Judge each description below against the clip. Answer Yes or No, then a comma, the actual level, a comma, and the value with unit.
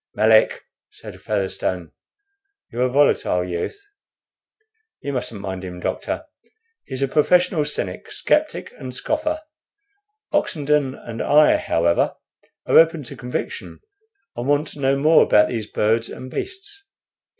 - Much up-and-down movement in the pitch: Yes, wide, 6.1 semitones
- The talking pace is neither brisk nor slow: No, slow, 130 wpm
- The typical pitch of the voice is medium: No, low, 130 Hz